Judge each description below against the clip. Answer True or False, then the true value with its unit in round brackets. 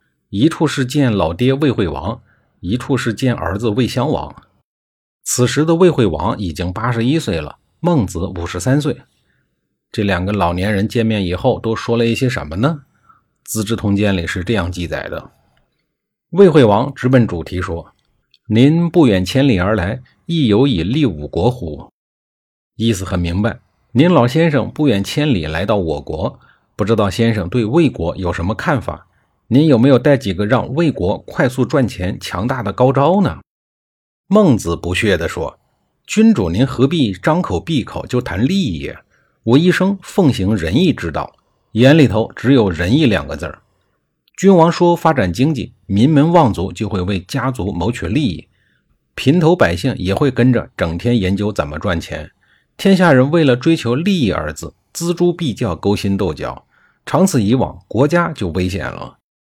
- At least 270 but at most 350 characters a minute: False (245 characters per minute)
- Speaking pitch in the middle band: False (115 Hz)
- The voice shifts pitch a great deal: True (6.4 semitones)